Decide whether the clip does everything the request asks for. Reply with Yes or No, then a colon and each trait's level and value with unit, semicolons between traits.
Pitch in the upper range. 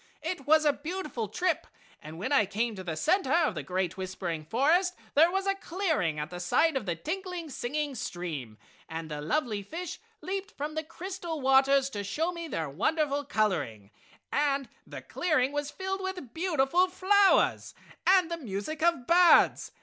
Yes: very high, 290 Hz